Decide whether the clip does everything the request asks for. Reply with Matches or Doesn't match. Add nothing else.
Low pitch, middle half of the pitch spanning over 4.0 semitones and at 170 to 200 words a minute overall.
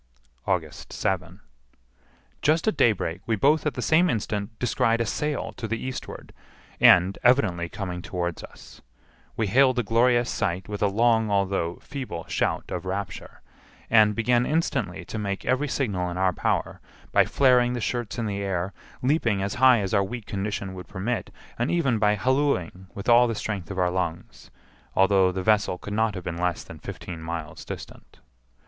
Matches